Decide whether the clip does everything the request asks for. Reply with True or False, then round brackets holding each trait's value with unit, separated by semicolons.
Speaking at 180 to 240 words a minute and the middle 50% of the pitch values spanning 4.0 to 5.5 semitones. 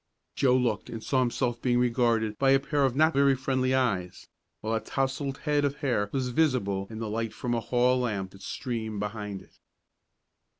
False (200 wpm; 3.4 semitones)